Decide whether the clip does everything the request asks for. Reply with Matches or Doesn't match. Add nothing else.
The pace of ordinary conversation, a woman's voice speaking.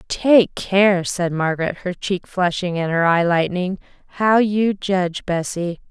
Matches